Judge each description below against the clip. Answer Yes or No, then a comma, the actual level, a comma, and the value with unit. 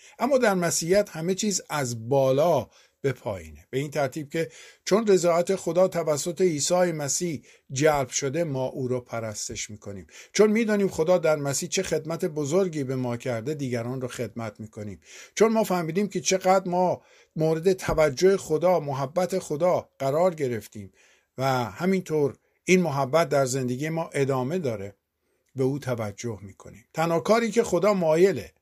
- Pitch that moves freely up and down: Yes, wide, 6.2 semitones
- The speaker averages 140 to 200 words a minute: Yes, average, 150 wpm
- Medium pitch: Yes, medium, 155 Hz